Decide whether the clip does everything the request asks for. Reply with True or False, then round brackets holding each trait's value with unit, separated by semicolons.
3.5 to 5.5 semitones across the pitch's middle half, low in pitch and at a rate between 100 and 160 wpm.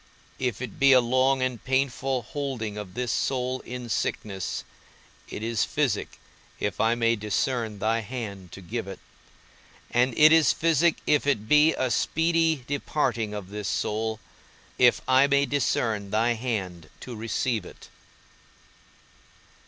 True (3.9 semitones; 120 Hz; 145 wpm)